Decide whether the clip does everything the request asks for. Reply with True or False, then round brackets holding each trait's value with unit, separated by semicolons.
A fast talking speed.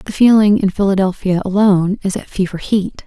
False (175 wpm)